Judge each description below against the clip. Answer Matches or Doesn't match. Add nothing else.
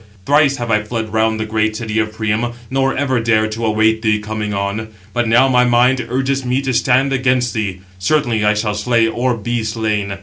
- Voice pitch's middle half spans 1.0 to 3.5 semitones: Matches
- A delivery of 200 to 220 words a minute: Matches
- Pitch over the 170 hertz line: Doesn't match